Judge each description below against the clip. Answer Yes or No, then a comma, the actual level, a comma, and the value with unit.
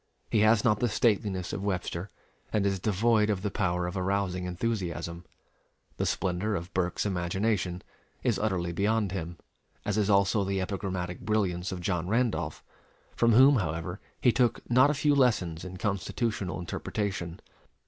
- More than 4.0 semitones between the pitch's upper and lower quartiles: No, average, 3.3 semitones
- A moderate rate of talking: Yes, average, 155 wpm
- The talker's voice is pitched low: Yes, low, 100 Hz